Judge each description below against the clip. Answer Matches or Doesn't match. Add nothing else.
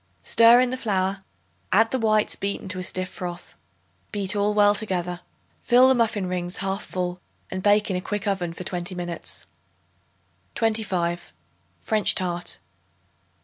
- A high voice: Matches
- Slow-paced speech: Doesn't match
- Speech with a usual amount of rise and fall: Matches